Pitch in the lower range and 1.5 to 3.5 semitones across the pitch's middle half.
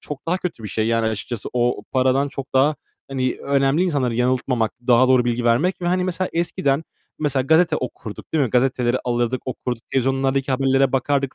Yes: low, 130 Hz; narrow, 2.5 semitones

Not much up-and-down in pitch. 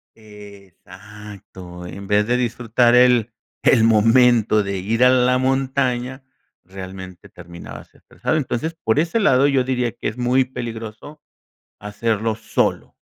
No: average, 3.6 semitones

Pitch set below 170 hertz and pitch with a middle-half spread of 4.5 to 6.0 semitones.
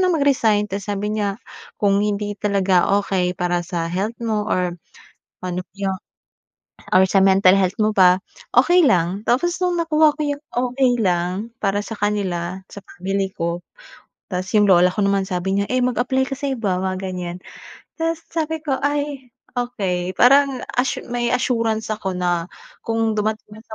No: high, 205 Hz; average, 5.0 semitones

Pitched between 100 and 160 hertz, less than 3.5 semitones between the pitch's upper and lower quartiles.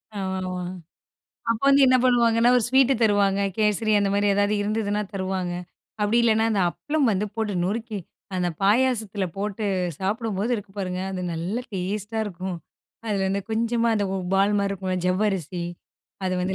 No: high, 205 Hz; average, 2.7 semitones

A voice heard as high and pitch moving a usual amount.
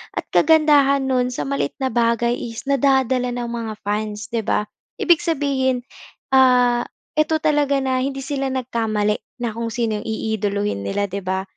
Yes: high, 245 Hz; average, 3.7 semitones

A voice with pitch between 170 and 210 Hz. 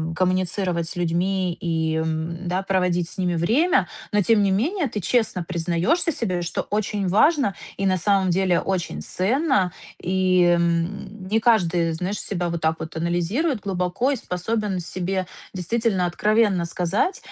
Yes: medium, 185 Hz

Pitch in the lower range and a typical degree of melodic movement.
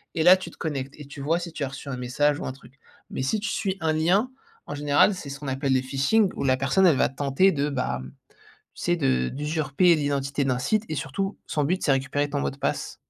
No: medium, 145 Hz; average, 3.7 semitones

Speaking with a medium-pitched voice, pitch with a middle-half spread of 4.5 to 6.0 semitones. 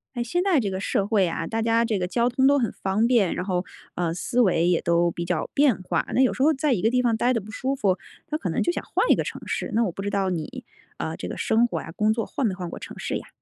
No: high, 220 Hz; average, 5.1 semitones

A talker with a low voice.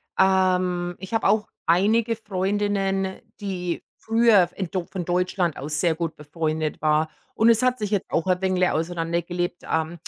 No: medium, 180 Hz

